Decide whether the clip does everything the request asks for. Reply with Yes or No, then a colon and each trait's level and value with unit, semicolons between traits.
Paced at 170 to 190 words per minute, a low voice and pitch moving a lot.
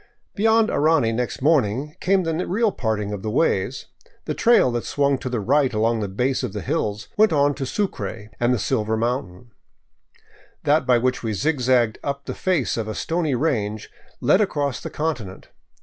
Yes: average, 180 wpm; low, 130 Hz; wide, 5.9 semitones